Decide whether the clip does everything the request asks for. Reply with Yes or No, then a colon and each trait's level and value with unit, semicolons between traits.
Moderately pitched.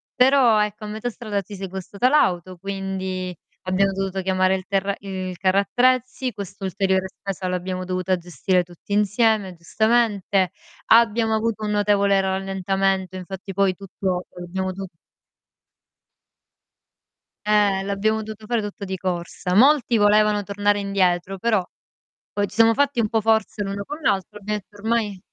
No: high, 200 Hz